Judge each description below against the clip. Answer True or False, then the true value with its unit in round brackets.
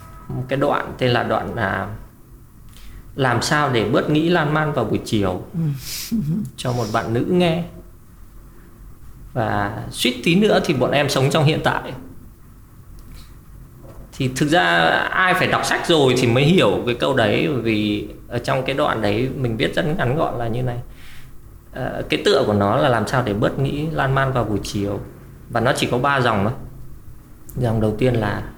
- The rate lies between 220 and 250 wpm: False (185 wpm)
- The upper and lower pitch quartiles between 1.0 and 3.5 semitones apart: False (4.0 semitones)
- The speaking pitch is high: False (120 Hz)